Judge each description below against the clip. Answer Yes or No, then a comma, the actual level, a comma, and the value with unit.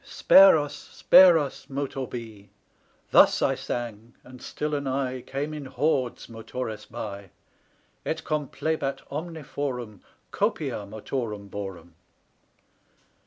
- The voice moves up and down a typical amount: Yes, average, 4.9 semitones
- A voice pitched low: Yes, low, 130 Hz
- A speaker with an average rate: No, slow, 110 wpm